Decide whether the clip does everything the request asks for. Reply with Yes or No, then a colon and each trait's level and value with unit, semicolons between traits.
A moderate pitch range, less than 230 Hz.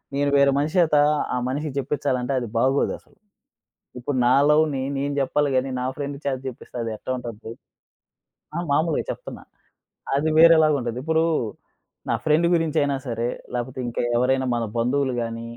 Yes: average, 3.3 semitones; medium, 140 Hz